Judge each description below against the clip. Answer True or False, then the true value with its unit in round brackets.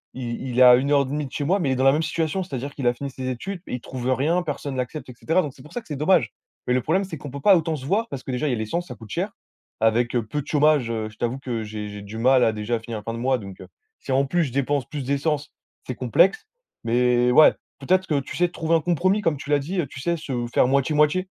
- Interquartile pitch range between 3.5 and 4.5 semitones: True (4.2 semitones)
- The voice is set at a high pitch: False (140 Hz)